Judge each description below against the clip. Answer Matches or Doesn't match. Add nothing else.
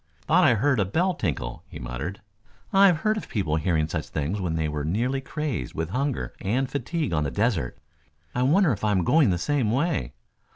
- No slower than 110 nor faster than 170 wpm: Doesn't match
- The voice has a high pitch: Doesn't match